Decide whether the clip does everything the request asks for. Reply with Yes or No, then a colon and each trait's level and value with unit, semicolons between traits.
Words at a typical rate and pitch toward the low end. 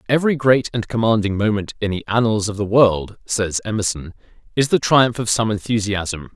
Yes: average, 180 wpm; low, 110 Hz